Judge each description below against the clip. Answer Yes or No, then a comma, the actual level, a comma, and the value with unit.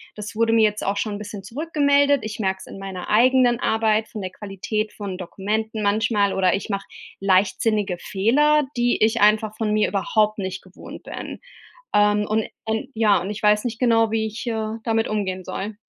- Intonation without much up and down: Yes, narrow, 2.0 semitones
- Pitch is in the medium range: No, high, 215 Hz